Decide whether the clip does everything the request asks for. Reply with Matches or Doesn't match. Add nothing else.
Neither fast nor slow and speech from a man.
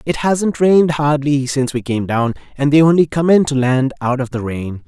Doesn't match